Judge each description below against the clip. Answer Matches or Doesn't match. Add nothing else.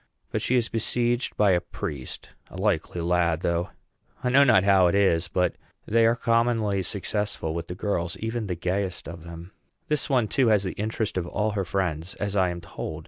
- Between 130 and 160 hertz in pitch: Doesn't match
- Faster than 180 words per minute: Matches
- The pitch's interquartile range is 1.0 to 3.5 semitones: Doesn't match